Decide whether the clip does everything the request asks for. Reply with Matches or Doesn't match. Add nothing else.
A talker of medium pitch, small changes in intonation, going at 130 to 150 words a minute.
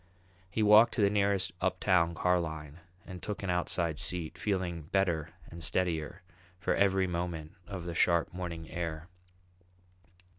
Doesn't match